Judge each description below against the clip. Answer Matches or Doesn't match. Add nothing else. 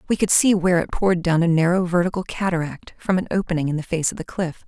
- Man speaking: Doesn't match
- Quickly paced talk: Matches